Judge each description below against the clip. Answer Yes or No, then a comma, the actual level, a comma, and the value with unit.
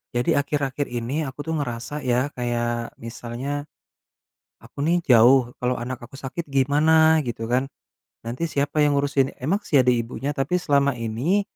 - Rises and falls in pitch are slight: No, average, 3.2 semitones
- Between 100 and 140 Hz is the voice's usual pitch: Yes, low, 135 Hz